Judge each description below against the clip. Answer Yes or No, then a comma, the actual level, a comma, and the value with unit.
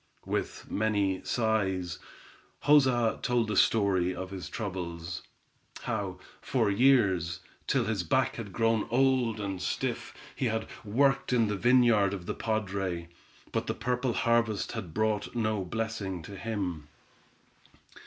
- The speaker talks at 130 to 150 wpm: Yes, slow, 135 wpm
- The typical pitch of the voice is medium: No, low, 105 Hz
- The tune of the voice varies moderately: Yes, average, 3.8 semitones